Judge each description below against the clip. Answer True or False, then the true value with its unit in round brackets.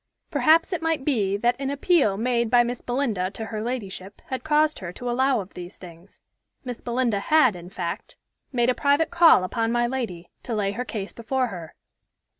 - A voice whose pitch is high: True (240 Hz)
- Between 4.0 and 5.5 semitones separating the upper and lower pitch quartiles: True (5.1 semitones)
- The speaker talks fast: False (195 wpm)